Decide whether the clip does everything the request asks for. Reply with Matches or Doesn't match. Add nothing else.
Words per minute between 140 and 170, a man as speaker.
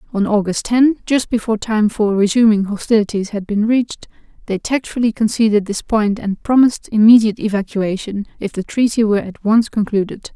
Doesn't match